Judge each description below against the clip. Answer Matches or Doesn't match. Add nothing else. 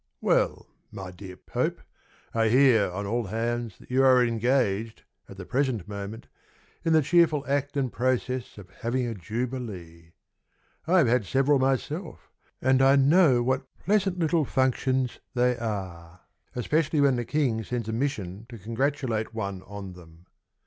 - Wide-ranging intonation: Doesn't match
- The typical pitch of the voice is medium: Doesn't match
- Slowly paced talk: Doesn't match